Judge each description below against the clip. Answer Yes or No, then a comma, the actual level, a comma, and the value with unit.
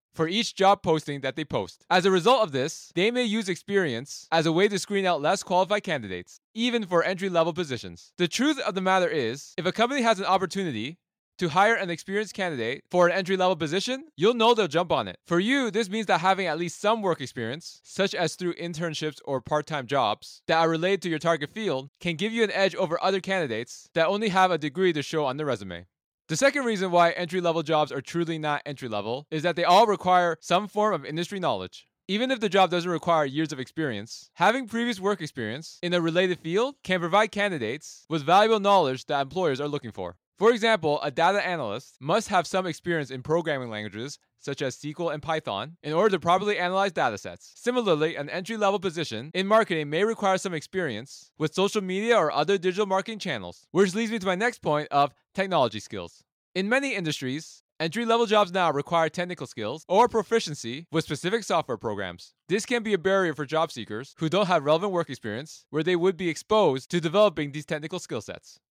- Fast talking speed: Yes, fast, 210 wpm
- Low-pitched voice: No, medium, 175 Hz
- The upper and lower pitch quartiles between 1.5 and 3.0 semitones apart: No, average, 4.6 semitones